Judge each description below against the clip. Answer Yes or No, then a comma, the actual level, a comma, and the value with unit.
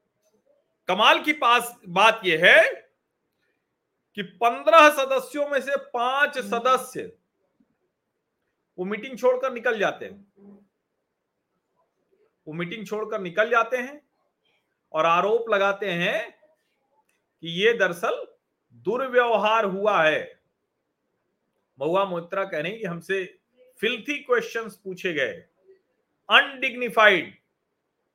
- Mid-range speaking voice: No, high, 235 Hz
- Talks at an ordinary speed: No, slow, 100 wpm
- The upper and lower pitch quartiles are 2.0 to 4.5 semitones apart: No, wide, 5.5 semitones